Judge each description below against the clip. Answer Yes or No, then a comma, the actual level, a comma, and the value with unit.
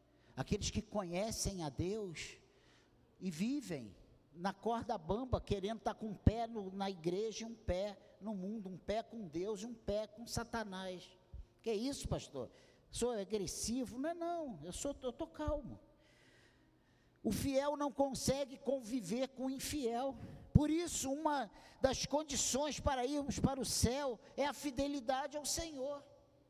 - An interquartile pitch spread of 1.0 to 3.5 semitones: No, average, 5.3 semitones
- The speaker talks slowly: No, average, 160 wpm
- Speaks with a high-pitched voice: Yes, high, 235 Hz